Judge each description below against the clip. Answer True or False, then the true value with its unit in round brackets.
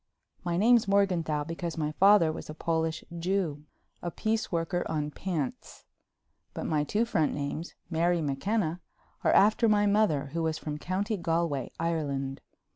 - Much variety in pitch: False (4.2 semitones)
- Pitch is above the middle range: False (165 Hz)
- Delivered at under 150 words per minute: True (140 wpm)